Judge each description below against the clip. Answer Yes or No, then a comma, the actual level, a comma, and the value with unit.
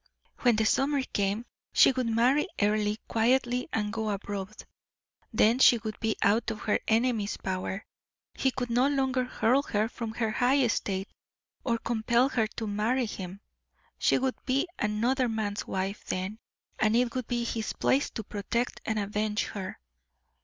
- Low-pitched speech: No, high, 225 Hz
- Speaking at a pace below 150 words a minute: No, average, 160 wpm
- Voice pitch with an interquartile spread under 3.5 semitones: Yes, average, 3.1 semitones